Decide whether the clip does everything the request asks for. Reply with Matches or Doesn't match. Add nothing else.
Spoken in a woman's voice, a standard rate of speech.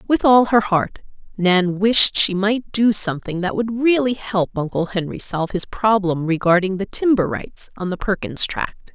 Matches